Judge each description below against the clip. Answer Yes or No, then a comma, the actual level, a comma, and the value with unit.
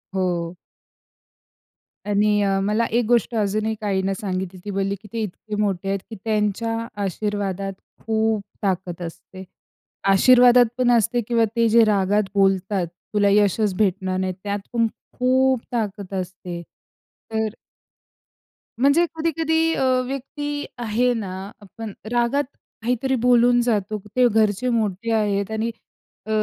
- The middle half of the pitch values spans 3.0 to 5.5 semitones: Yes, average, 3.4 semitones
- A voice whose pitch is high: Yes, high, 215 Hz